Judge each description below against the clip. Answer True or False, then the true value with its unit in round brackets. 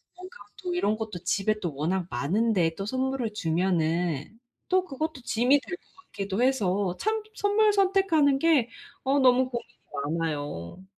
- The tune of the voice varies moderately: False (8.2 semitones)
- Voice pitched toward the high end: True (225 Hz)